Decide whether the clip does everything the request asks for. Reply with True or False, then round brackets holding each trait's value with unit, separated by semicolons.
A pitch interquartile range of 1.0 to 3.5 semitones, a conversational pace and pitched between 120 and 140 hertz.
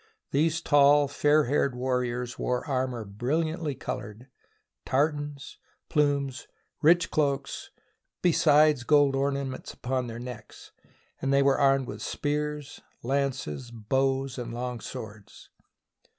False (2.8 semitones; 115 wpm; 135 Hz)